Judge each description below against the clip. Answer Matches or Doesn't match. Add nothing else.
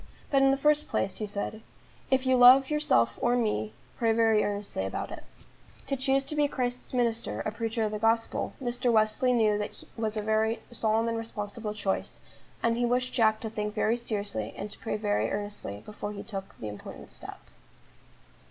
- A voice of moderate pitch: Doesn't match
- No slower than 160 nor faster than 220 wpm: Matches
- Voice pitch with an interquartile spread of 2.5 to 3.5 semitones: Matches